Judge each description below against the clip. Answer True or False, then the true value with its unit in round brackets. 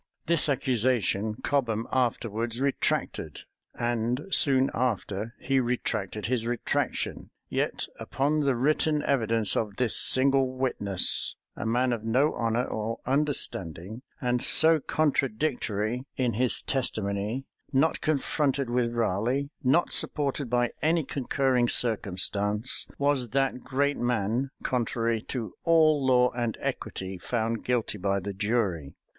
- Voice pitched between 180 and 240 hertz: False (120 Hz)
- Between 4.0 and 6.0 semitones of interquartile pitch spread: False (3.5 semitones)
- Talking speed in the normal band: False (120 wpm)